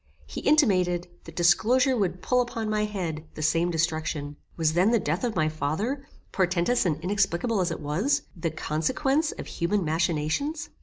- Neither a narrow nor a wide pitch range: No, wide, 6.2 semitones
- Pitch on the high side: No, medium, 180 Hz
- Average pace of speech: Yes, average, 165 wpm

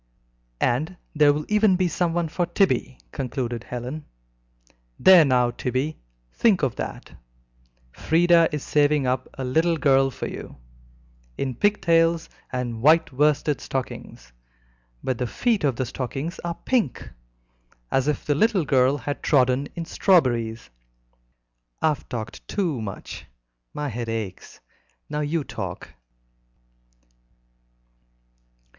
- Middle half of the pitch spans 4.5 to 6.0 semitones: Yes, average, 4.8 semitones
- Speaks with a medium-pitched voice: Yes, medium, 145 Hz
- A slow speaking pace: Yes, slow, 125 wpm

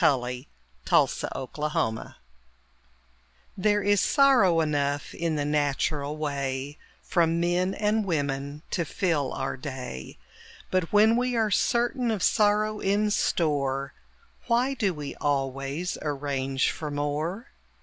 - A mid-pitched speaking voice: Yes, medium, 155 Hz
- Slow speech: Yes, slow, 125 wpm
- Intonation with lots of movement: Yes, wide, 6.5 semitones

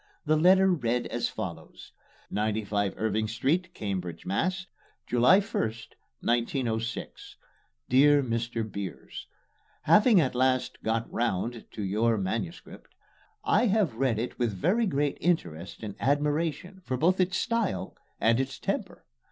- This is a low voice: Yes, low, 120 Hz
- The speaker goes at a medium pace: No, slow, 125 wpm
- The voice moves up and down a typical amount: No, wide, 6.8 semitones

